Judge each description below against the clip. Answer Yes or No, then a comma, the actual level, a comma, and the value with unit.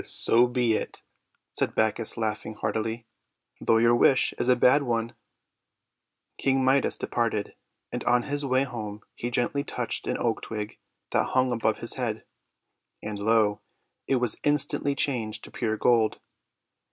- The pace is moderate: Yes, average, 150 wpm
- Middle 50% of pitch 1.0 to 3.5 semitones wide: Yes, narrow, 2.6 semitones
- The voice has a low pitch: Yes, low, 120 Hz